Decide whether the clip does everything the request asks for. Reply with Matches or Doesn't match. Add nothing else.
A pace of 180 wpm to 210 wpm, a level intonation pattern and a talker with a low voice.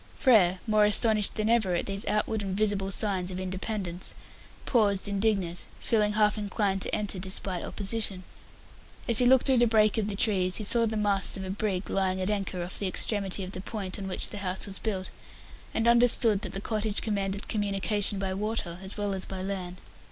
Doesn't match